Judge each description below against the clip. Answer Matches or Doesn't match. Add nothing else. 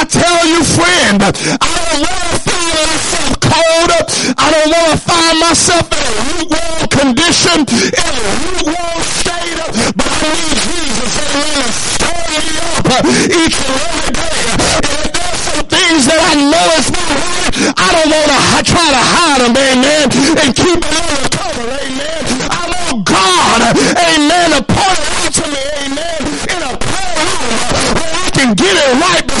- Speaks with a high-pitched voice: Matches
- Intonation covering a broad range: Doesn't match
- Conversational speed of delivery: Matches